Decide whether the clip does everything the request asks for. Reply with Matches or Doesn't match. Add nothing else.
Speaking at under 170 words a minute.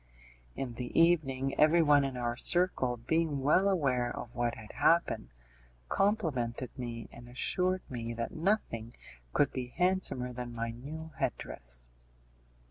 Matches